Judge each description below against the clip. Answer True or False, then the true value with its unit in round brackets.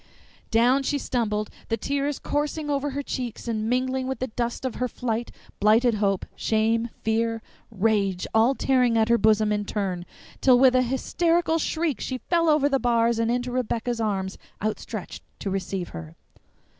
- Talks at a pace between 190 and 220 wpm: False (165 wpm)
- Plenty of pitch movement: False (3.4 semitones)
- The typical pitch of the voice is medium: False (235 Hz)